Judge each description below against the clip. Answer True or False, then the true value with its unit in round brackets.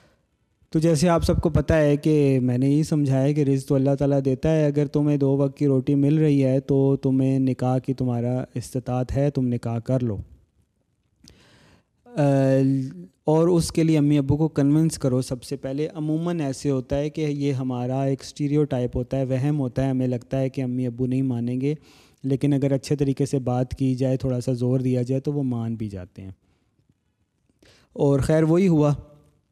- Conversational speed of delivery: False (200 wpm)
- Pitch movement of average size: False (2.3 semitones)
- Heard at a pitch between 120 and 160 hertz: True (135 Hz)